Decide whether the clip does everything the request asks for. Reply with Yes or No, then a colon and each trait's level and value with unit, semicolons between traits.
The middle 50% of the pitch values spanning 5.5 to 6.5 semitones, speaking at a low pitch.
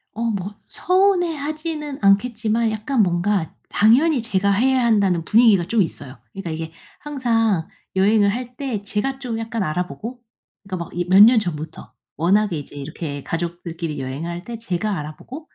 No: wide, 5.8 semitones; high, 205 Hz